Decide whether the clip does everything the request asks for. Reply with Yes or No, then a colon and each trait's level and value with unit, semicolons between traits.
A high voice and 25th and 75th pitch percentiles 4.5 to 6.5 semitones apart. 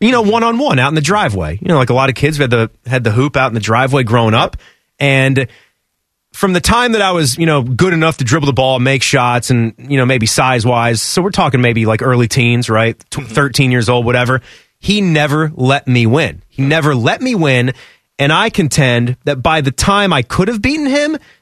No: low, 135 Hz; average, 4.8 semitones